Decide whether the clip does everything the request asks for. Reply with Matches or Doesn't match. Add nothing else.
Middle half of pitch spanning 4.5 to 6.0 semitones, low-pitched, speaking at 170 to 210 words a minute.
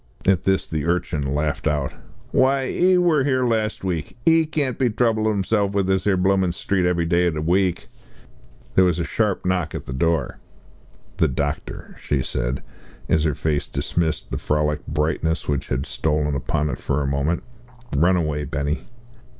Matches